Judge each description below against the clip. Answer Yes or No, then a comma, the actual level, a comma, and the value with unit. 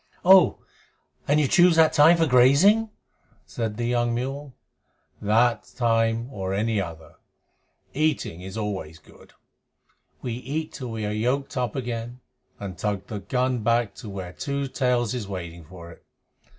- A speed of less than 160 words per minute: Yes, average, 150 wpm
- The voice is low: Yes, low, 120 Hz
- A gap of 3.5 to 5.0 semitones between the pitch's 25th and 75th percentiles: Yes, average, 4.7 semitones